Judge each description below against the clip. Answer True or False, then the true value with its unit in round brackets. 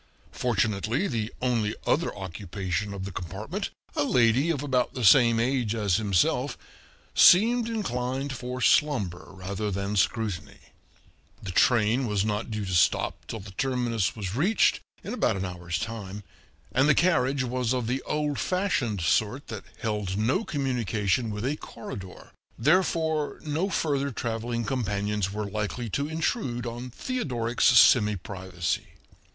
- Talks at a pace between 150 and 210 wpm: False (140 wpm)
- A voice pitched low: True (115 Hz)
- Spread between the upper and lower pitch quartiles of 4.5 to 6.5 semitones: True (4.9 semitones)